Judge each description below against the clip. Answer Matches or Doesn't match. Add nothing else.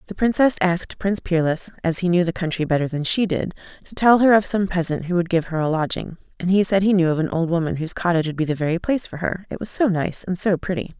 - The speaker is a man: Doesn't match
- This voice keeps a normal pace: Doesn't match